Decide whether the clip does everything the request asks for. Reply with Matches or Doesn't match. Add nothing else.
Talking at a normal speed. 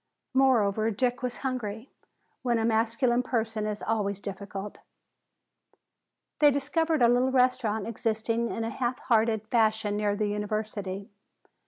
Doesn't match